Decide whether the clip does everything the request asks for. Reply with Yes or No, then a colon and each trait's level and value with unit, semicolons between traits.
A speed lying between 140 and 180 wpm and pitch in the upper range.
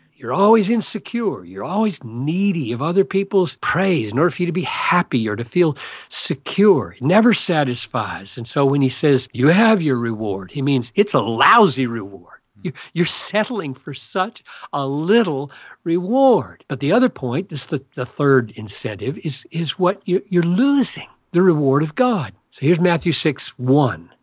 No: average, 170 wpm; medium, 155 Hz